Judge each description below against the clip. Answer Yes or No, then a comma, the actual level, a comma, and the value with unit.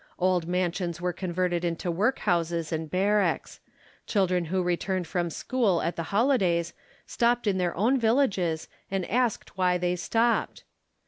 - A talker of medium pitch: Yes, medium, 180 Hz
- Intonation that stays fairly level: No, average, 3.2 semitones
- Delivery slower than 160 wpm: Yes, average, 140 wpm